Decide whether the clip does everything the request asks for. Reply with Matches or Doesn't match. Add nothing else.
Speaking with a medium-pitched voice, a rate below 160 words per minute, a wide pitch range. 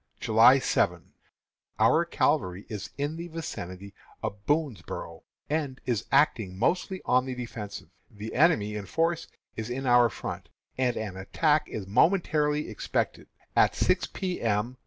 Doesn't match